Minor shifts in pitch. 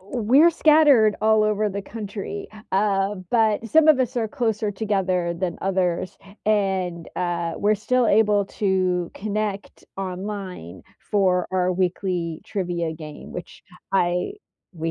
No: average, 3.0 semitones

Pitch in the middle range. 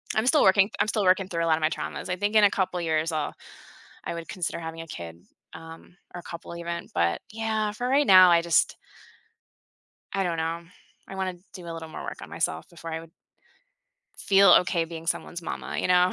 Yes: medium, 175 Hz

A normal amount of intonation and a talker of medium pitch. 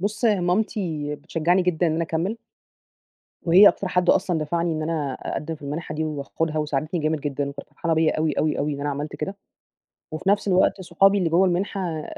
Yes: average, 3.0 semitones; medium, 165 Hz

